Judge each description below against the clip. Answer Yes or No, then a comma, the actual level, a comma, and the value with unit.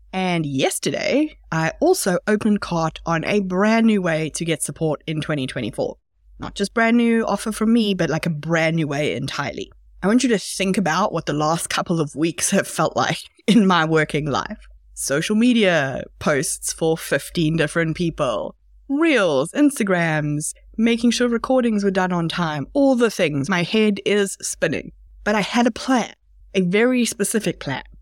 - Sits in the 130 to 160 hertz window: No, high, 190 Hz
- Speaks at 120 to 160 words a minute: No, average, 175 wpm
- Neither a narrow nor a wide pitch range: No, wide, 5.7 semitones